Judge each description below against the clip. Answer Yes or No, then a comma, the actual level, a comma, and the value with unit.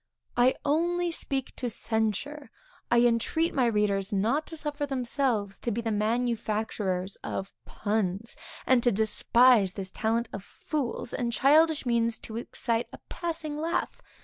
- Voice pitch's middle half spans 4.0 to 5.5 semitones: Yes, average, 4.8 semitones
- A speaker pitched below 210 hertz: No, high, 235 Hz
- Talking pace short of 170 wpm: Yes, average, 145 wpm